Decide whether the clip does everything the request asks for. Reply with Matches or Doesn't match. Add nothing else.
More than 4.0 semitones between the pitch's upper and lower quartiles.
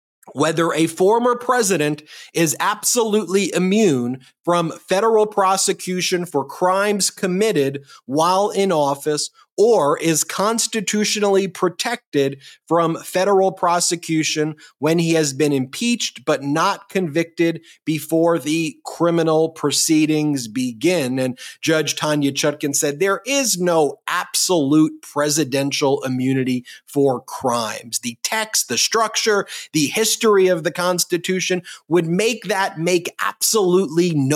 Matches